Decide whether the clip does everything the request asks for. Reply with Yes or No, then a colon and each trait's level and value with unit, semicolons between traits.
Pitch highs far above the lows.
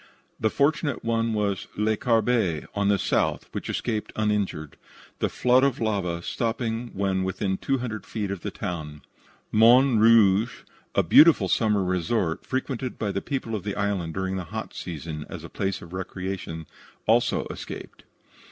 No: average, 3.5 semitones